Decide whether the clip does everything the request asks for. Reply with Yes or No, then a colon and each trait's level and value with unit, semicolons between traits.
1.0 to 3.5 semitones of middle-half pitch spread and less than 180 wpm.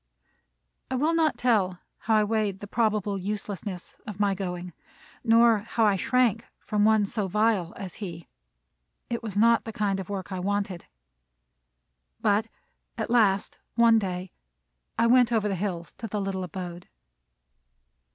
Yes: average, 3.0 semitones; average, 150 wpm